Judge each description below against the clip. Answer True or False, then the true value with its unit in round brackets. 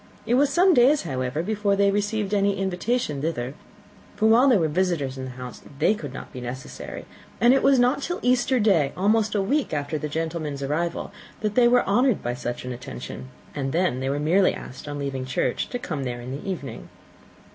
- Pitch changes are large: True (8.2 semitones)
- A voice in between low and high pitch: True (175 Hz)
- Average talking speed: False (210 wpm)